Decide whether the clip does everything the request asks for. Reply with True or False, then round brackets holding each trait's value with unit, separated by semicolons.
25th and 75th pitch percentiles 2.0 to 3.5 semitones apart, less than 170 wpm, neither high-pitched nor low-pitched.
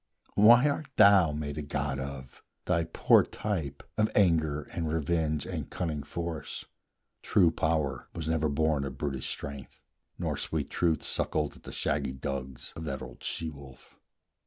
False (3.1 semitones; 160 wpm; 75 Hz)